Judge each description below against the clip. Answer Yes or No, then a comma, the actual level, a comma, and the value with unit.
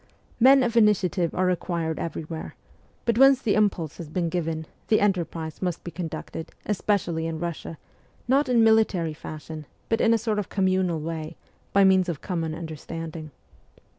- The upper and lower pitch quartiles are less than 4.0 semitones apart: No, average, 4.4 semitones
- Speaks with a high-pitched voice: No, medium, 175 Hz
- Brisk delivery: No, average, 160 wpm